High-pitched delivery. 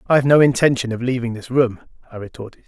No: low, 125 Hz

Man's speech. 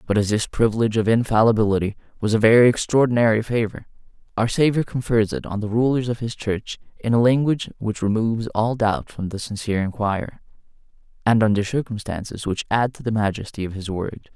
Yes: male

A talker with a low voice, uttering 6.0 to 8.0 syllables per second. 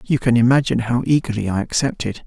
Yes: low, 120 Hz; 6.5 syllables/s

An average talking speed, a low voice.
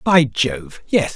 Yes: average, 155 wpm; low, 130 Hz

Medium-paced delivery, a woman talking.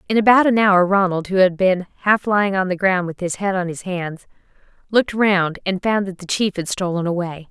No: fast, 230 wpm; female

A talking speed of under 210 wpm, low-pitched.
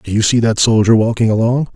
No: fast, 240 wpm; low, 115 Hz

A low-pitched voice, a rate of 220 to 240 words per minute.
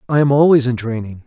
Yes: low, 130 Hz; fast, 235 wpm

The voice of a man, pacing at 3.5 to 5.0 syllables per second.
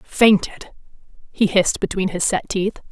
No: female; 4.5 syllables/s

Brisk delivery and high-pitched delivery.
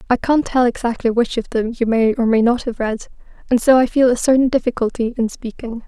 Yes: fast, 235 wpm; high, 240 Hz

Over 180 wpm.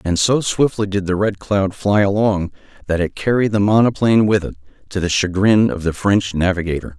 Yes: average, 200 wpm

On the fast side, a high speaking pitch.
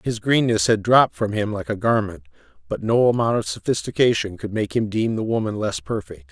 No: fast, 210 wpm; low, 110 Hz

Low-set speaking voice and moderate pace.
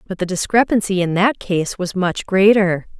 No: high, 190 Hz; average, 180 wpm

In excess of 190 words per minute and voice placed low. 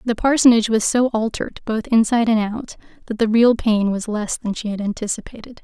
No: average, 200 wpm; high, 225 Hz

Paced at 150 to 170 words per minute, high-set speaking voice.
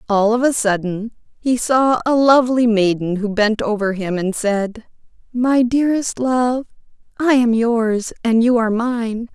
Yes: average, 160 wpm; high, 230 Hz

